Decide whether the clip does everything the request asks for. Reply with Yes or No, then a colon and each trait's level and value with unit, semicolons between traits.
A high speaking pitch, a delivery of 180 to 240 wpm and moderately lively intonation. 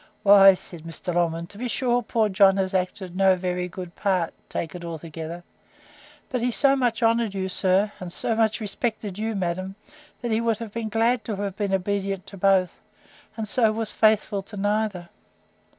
Yes: high, 195 Hz; average, 185 wpm; average, 3.3 semitones